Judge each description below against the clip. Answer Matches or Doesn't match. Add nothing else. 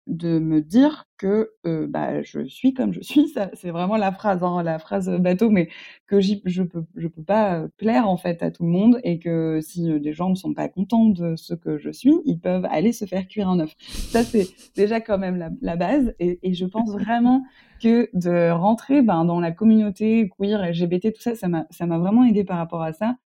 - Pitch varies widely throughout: Doesn't match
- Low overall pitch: Doesn't match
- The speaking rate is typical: Doesn't match